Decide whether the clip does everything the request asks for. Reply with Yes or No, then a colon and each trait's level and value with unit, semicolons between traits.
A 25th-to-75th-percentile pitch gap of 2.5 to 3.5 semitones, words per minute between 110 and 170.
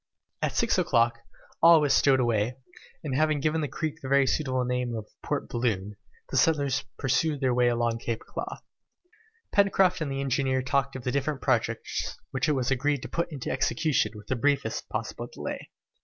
No: average, 3.2 semitones; average, 185 wpm